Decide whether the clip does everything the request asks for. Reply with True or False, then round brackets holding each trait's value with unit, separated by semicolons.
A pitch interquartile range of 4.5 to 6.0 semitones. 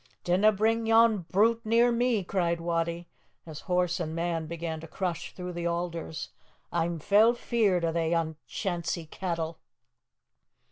False (3.8 semitones)